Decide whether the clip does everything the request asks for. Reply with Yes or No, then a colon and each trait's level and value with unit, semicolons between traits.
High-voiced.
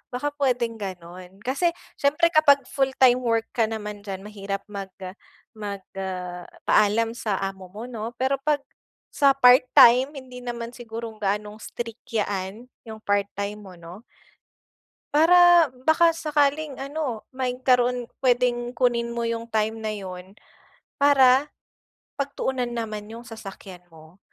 Yes: high, 235 Hz